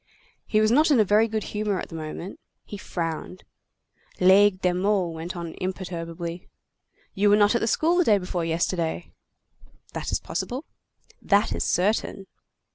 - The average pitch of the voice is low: No, high, 190 Hz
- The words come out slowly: No, average, 160 wpm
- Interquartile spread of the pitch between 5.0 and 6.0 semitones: No, average, 3.5 semitones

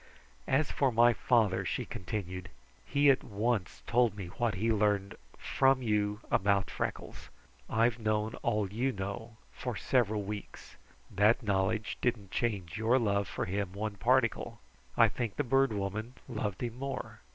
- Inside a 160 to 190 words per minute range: No, average, 150 wpm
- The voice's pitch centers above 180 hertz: No, low, 110 Hz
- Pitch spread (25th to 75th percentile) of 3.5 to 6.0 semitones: No, average, 3.1 semitones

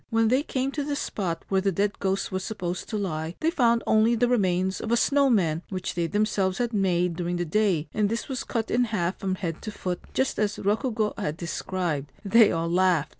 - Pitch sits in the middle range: No, high, 200 Hz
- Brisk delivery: Yes, fast, 225 wpm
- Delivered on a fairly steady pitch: No, average, 4.3 semitones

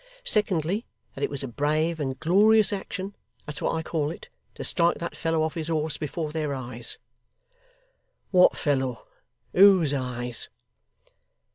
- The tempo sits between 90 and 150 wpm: Yes, average, 145 wpm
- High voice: No, medium, 155 Hz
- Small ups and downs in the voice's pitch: No, average, 3.9 semitones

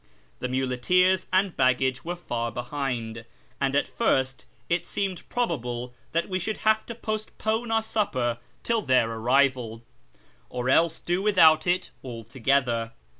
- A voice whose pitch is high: No, medium, 140 Hz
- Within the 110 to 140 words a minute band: Yes, slow, 135 wpm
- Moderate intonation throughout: No, wide, 7.0 semitones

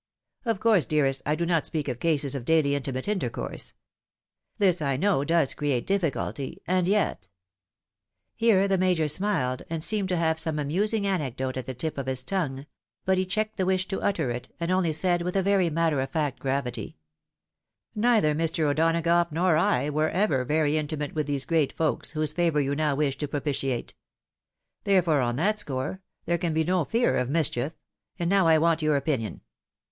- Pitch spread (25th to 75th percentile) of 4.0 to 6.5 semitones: Yes, average, 4.7 semitones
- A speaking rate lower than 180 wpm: No, average, 195 wpm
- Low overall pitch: No, medium, 160 Hz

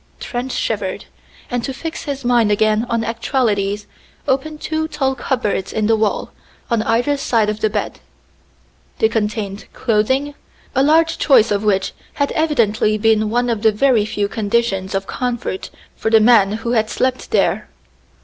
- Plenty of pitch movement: No, average, 3.7 semitones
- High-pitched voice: Yes, high, 225 Hz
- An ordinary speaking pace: Yes, average, 160 wpm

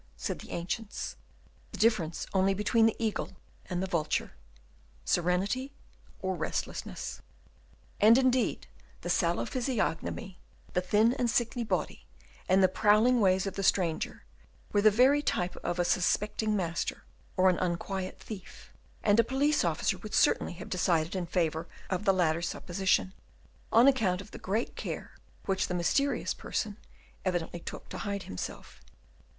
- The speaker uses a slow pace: No, average, 150 wpm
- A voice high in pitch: Yes, high, 195 Hz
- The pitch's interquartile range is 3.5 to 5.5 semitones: Yes, average, 3.8 semitones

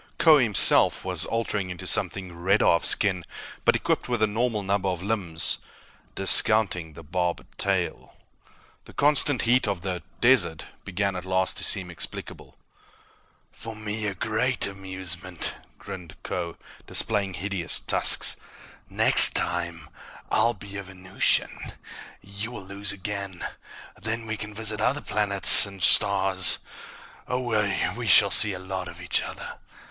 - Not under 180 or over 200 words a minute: No, average, 140 wpm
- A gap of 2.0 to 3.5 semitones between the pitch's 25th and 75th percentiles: Yes, average, 2.8 semitones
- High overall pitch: No, low, 100 Hz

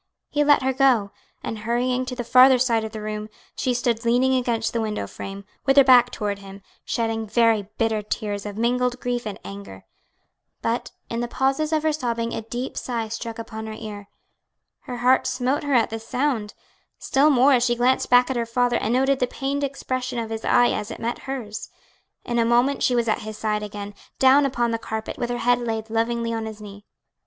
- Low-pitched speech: No, high, 235 Hz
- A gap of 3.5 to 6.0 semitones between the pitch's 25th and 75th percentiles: No, narrow, 2.6 semitones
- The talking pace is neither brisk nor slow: No, fast, 215 wpm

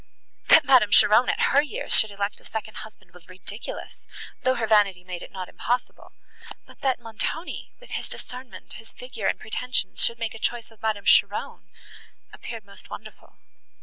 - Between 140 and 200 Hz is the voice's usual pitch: No, high, 225 Hz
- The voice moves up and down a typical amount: Yes, average, 3.6 semitones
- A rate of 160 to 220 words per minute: Yes, average, 170 wpm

